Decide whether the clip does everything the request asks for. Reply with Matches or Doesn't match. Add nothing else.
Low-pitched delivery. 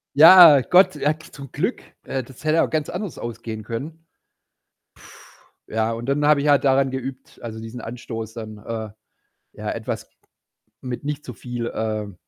Matches